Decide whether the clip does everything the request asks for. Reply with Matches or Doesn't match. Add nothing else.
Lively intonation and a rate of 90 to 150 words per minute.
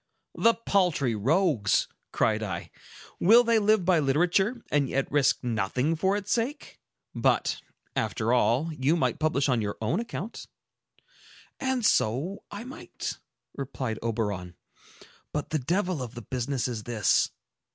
Matches